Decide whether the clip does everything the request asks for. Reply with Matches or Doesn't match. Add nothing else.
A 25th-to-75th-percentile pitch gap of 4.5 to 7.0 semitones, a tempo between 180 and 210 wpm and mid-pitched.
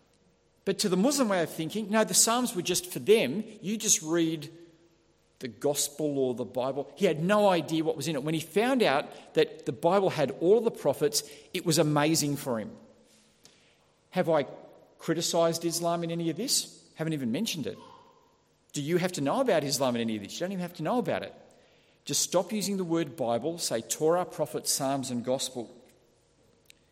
Matches